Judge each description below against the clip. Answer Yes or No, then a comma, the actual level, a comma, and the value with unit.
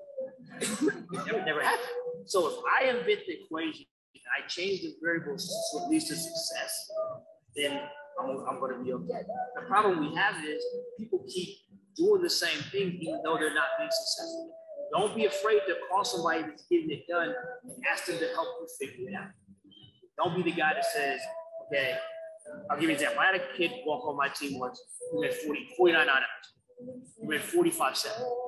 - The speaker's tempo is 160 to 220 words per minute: Yes, average, 195 wpm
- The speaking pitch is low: No, very high, 290 Hz